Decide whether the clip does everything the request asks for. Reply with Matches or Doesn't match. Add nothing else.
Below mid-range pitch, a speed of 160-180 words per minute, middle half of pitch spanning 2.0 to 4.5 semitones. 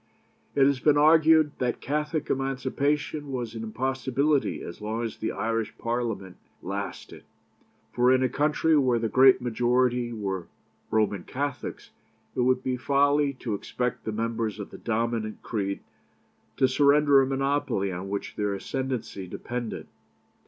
Doesn't match